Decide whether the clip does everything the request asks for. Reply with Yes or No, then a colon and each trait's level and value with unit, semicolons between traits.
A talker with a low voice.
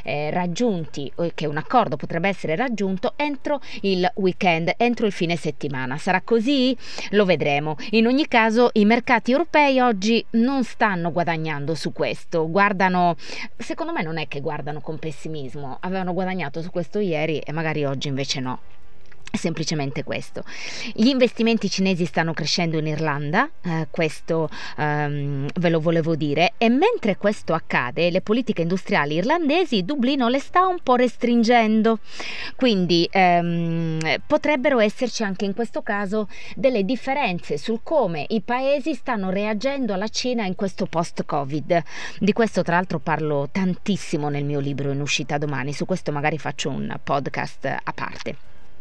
No: medium, 185 Hz